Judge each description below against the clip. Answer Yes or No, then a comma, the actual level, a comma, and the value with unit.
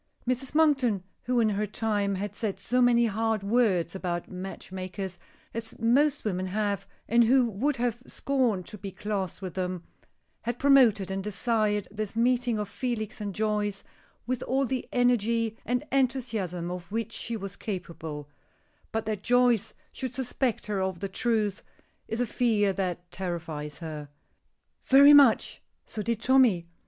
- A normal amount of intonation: Yes, average, 4.1 semitones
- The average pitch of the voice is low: No, high, 215 Hz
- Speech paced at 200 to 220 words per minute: No, average, 155 wpm